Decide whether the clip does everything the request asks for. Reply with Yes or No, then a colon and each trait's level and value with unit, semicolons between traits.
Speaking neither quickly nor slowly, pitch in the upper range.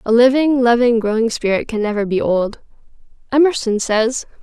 Yes: average, 150 wpm; high, 235 Hz